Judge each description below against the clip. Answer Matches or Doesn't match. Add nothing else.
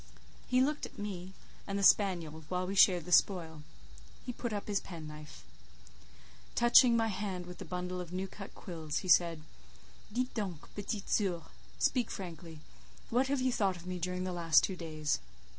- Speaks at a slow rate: Doesn't match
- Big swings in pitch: Doesn't match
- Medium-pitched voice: Matches